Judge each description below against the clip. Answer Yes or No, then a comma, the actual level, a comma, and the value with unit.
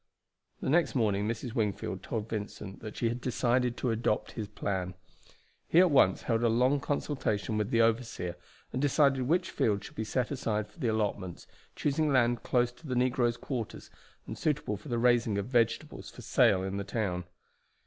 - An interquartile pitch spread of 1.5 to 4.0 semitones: Yes, average, 3.5 semitones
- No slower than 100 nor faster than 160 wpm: No, average, 185 wpm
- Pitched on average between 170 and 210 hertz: No, low, 115 Hz